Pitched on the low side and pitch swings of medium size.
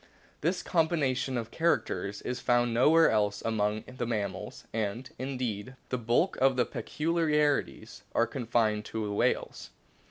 Yes: low, 120 Hz; average, 4.5 semitones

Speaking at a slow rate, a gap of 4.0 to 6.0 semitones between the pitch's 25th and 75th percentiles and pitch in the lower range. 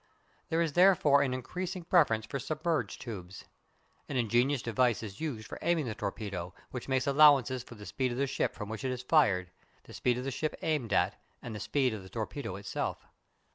No: fast, 205 wpm; average, 5.0 semitones; low, 125 Hz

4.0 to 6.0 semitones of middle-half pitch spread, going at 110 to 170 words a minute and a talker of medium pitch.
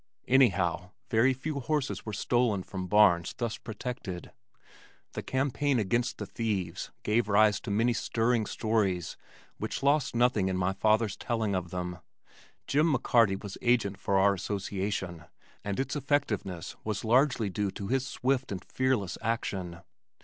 No: average, 4.3 semitones; average, 145 wpm; low, 110 Hz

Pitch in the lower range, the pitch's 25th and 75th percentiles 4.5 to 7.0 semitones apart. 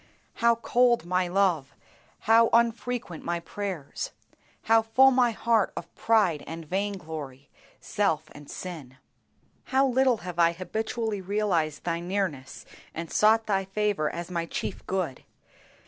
No: high, 190 Hz; average, 5.1 semitones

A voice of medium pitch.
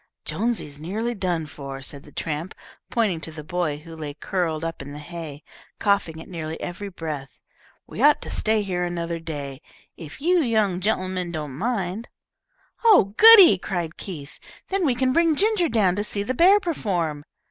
Yes: medium, 180 Hz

